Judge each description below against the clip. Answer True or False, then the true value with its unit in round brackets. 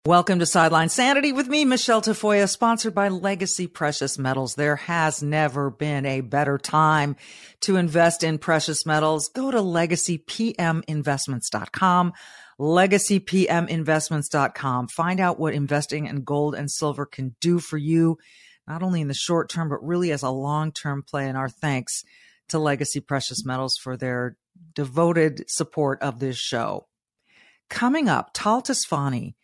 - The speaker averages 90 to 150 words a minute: True (145 wpm)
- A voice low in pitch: False (155 Hz)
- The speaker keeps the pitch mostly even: False (3.7 semitones)